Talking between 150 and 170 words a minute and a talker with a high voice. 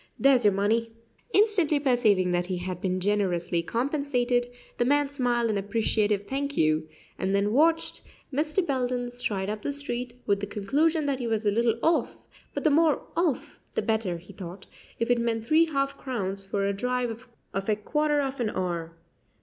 No: average, 180 wpm; high, 235 Hz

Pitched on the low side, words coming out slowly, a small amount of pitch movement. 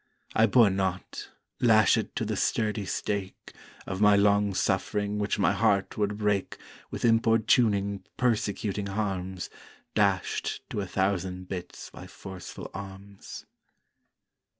Yes: low, 100 Hz; slow, 120 wpm; narrow, 1.7 semitones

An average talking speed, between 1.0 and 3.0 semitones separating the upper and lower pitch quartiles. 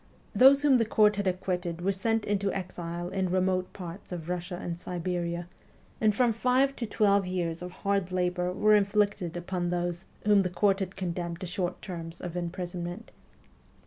Yes: average, 175 wpm; narrow, 2.5 semitones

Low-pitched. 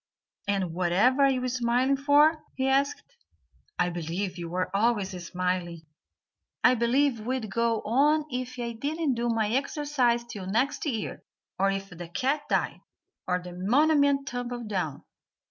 No: high, 235 Hz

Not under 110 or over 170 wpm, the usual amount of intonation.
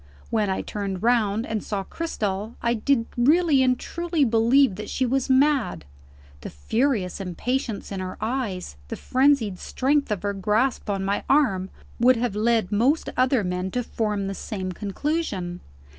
Yes: average, 160 wpm; average, 5.0 semitones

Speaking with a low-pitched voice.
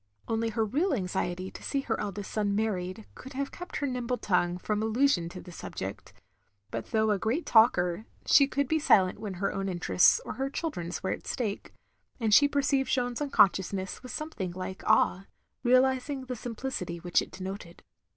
No: high, 220 Hz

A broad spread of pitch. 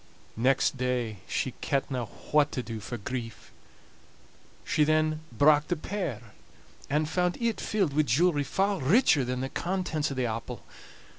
No: average, 4.4 semitones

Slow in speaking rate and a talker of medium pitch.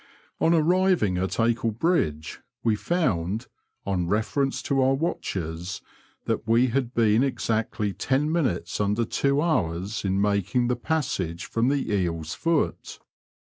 No: slow, 130 wpm; low, 115 Hz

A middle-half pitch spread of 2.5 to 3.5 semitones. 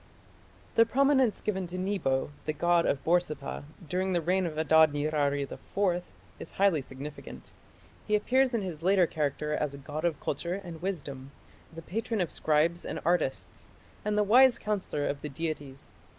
No: average, 4.7 semitones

